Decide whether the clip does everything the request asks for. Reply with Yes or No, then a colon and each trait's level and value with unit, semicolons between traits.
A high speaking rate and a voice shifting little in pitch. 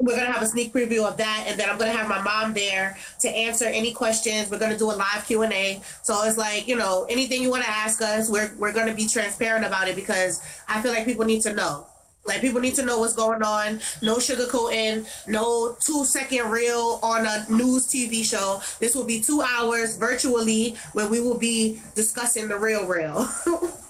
Yes: fast, 225 wpm; narrow, 1.9 semitones